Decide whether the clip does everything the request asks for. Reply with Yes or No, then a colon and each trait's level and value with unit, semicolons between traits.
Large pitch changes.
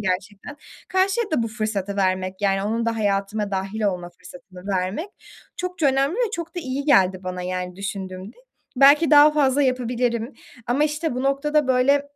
Yes: wide, 6.8 semitones